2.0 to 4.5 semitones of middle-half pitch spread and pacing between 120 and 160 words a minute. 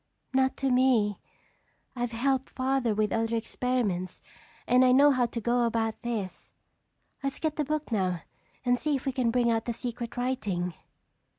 No: average, 2.7 semitones; average, 170 wpm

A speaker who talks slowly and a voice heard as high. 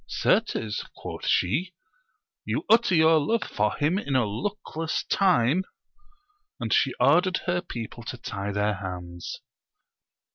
No: slow, 130 wpm; medium, 140 Hz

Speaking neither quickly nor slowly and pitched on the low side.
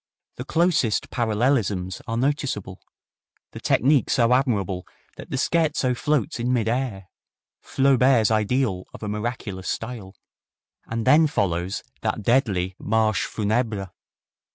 No: slow, 120 wpm; low, 115 Hz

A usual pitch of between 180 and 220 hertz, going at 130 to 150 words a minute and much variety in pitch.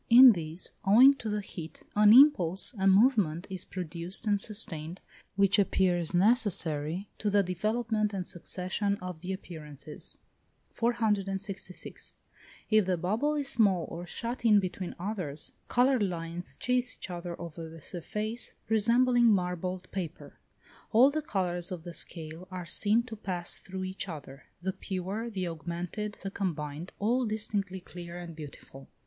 No: high, 190 Hz; average, 145 wpm; average, 3.7 semitones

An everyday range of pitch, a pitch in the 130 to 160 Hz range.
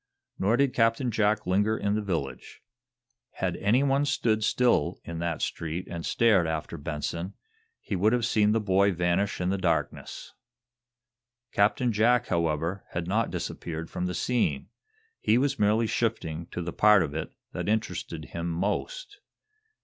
No: average, 4.9 semitones; low, 100 Hz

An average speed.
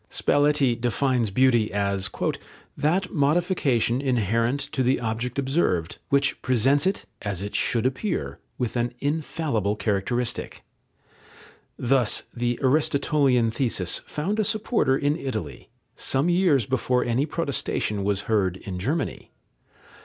No: slow, 120 wpm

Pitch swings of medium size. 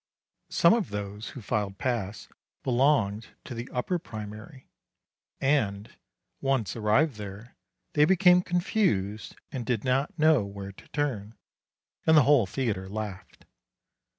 No: wide, 6.1 semitones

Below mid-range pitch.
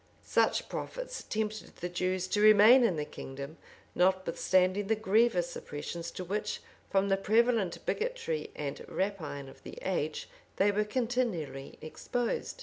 No: high, 195 Hz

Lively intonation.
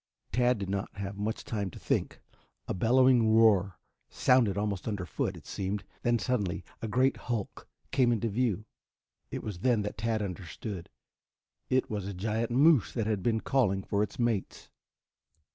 No: average, 3.2 semitones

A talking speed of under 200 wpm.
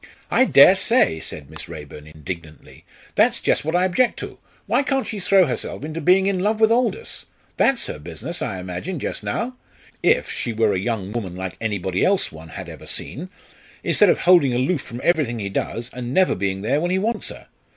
No: fast, 205 wpm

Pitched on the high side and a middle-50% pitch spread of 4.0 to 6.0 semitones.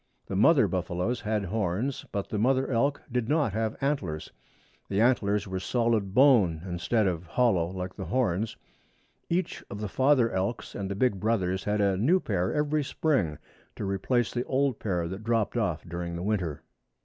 No: low, 105 Hz; average, 4.9 semitones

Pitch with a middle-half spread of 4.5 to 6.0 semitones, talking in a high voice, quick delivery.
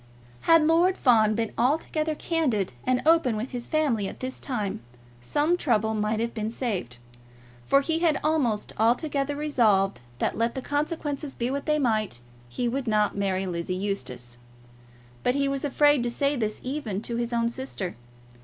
No: wide, 5.4 semitones; high, 240 Hz; average, 170 wpm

